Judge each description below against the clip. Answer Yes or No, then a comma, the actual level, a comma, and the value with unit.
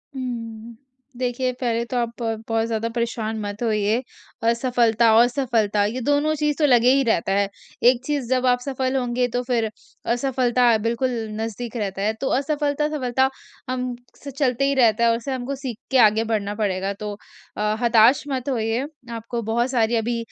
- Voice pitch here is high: Yes, high, 235 Hz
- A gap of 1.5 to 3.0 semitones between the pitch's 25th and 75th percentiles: Yes, narrow, 2.5 semitones